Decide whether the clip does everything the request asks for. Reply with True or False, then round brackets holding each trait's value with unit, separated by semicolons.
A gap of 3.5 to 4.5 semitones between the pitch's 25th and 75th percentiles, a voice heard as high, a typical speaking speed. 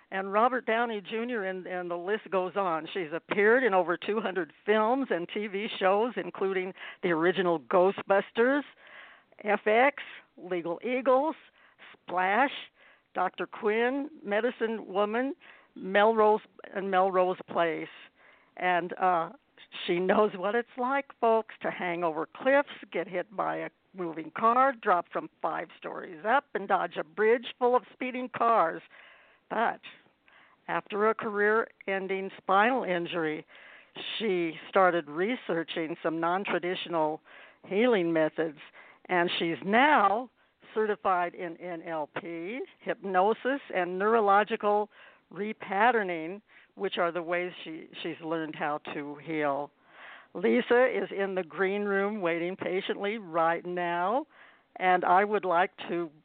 False (4.2 semitones; 195 Hz; 125 wpm)